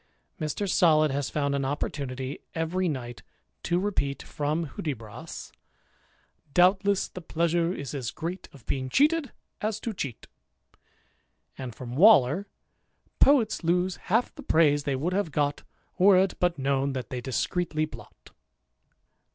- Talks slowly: No, average, 145 wpm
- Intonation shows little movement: No, average, 4.9 semitones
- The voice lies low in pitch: No, medium, 155 Hz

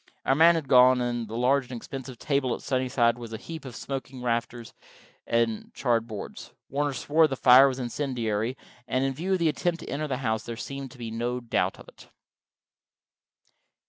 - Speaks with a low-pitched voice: Yes, low, 125 Hz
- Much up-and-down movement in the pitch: No, average, 2.7 semitones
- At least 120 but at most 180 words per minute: No, average, 195 wpm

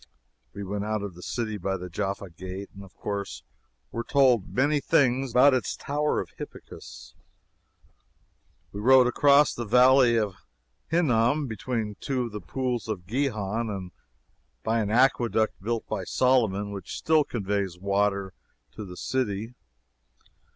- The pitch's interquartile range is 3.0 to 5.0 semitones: Yes, average, 4.3 semitones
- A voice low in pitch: Yes, low, 110 Hz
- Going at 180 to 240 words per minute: No, average, 145 wpm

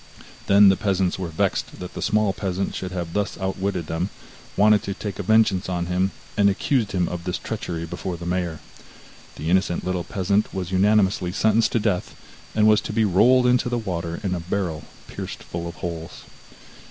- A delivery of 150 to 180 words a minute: No, average, 190 wpm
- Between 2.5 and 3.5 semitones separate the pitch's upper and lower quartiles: Yes, average, 2.8 semitones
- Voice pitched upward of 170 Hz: No, very low, 95 Hz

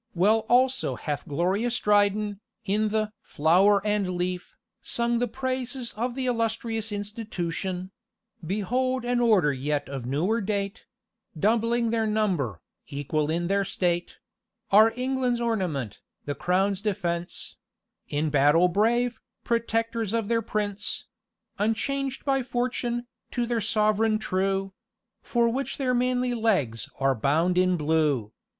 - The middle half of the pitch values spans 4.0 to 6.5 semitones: Yes, average, 5.0 semitones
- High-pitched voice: Yes, high, 210 Hz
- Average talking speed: No, slow, 130 wpm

